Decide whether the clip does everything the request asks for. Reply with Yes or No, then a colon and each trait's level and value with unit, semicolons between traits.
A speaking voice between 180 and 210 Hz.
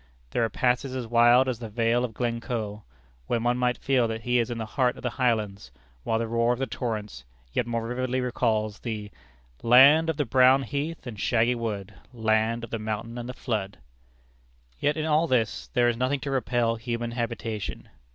No: low, 120 Hz